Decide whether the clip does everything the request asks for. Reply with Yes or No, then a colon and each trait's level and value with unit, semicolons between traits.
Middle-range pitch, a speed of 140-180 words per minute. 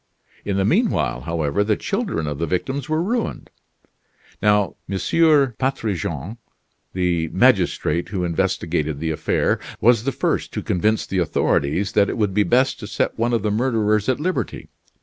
No: low, 105 Hz; average, 165 wpm